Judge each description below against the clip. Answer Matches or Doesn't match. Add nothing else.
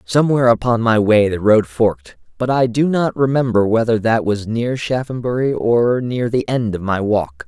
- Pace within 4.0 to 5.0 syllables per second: Matches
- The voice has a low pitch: Matches